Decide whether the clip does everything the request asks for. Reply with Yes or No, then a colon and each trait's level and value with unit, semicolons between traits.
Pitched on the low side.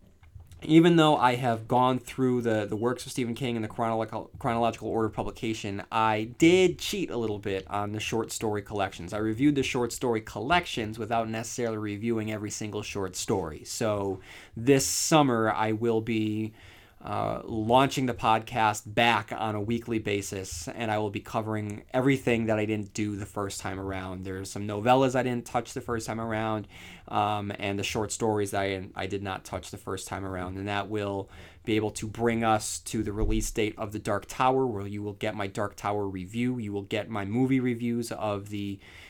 Yes: low, 110 Hz